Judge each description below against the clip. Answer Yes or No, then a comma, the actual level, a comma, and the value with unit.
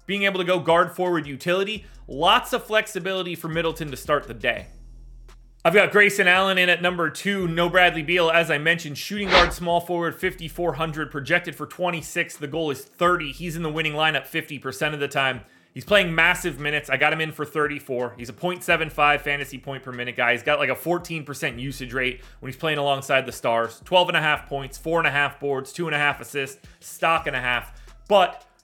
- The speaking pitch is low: No, medium, 160 Hz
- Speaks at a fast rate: Yes, fast, 215 wpm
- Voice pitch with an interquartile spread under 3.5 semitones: No, average, 4.1 semitones